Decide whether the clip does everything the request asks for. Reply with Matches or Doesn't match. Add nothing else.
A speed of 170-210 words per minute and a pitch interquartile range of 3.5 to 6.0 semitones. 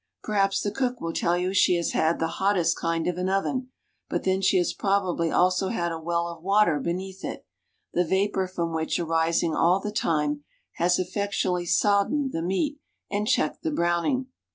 Doesn't match